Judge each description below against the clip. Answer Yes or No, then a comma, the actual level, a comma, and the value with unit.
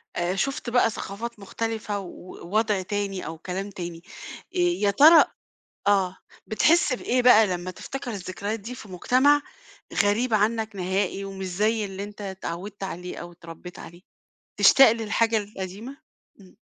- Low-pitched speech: No, high, 205 Hz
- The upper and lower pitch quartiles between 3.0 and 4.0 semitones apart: Yes, average, 3.5 semitones